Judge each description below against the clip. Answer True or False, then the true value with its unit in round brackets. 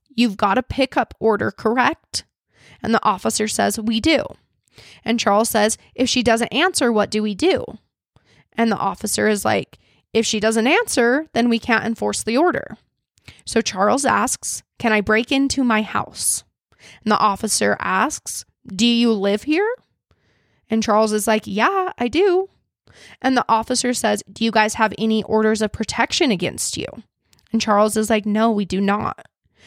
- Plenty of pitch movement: False (2.5 semitones)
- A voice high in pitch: True (225 Hz)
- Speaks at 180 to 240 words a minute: False (170 wpm)